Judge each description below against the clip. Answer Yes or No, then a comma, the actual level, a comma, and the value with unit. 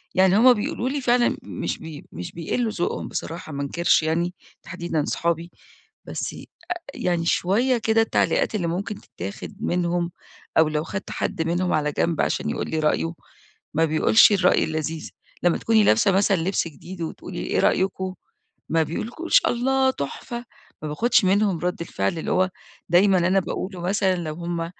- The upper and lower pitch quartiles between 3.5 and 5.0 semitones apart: Yes, average, 3.8 semitones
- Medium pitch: Yes, medium, 175 Hz